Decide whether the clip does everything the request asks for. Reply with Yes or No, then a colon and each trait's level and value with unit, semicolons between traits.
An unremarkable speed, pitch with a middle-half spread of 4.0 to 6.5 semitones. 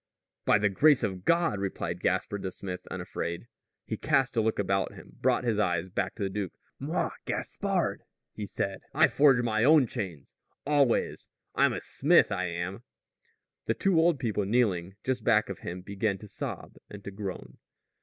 Yes: average, 175 wpm; average, 4.6 semitones